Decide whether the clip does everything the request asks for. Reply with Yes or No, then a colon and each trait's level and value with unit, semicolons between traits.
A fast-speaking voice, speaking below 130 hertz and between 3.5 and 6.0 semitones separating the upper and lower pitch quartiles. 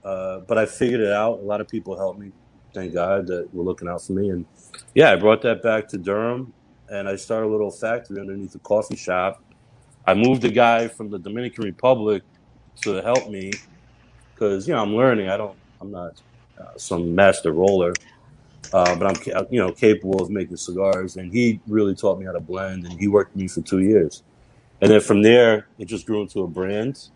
No: fast, 215 wpm; low, 105 Hz; average, 2.9 semitones